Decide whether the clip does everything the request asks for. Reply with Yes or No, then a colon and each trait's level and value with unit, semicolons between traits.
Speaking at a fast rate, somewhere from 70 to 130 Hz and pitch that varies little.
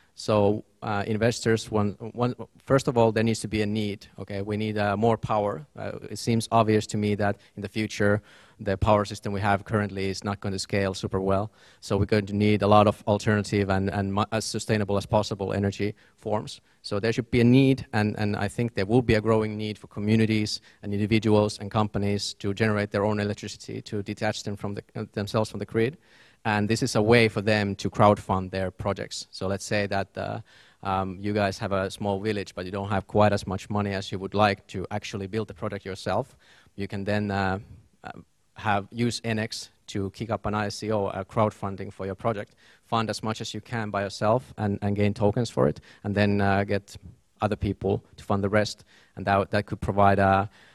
Yes: fast, 220 wpm; low, 105 Hz; narrow, 1.6 semitones